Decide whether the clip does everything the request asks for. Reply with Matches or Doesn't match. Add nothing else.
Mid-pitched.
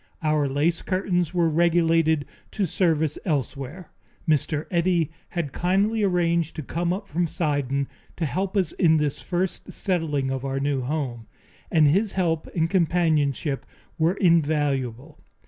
Matches